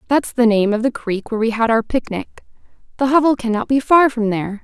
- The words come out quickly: Yes, fast, 245 wpm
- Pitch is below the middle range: No, high, 235 Hz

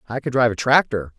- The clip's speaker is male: Yes, male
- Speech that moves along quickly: Yes, fast, 255 wpm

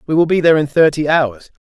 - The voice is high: No, medium, 150 Hz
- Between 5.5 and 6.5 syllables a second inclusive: Yes, 6.4 syllables/s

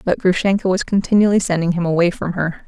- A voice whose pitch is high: No, medium, 180 Hz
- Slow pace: No, average, 200 wpm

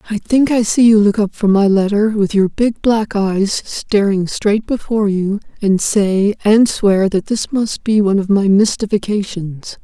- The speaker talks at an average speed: Yes, average, 190 wpm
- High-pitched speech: Yes, high, 205 Hz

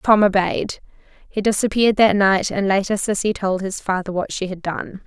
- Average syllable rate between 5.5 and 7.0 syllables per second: No, 5.1 syllables/s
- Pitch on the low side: No, high, 195 Hz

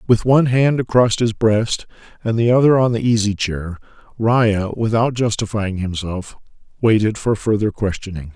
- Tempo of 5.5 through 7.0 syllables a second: No, 4.8 syllables/s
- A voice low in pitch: Yes, low, 110 Hz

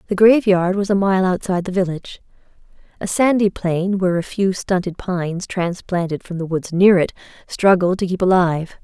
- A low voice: No, medium, 185 Hz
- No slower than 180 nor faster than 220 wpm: No, average, 170 wpm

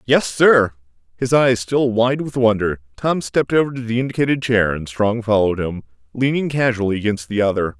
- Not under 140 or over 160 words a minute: No, average, 185 wpm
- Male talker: Yes, male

